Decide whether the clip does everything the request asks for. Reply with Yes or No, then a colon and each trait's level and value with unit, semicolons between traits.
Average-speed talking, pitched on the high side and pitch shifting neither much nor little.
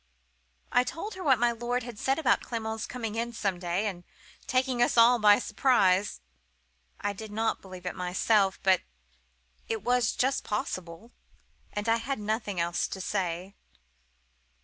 Yes: average, 150 wpm; high, 220 Hz; average, 4.1 semitones